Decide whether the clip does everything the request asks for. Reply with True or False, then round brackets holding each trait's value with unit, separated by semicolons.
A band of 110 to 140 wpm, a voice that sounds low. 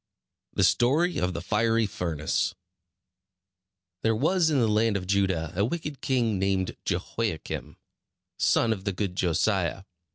True (135 wpm; 105 Hz)